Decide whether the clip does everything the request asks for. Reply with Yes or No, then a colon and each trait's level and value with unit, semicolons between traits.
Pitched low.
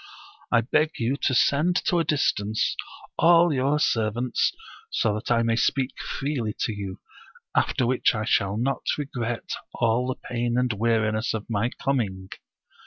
Yes: low, 120 Hz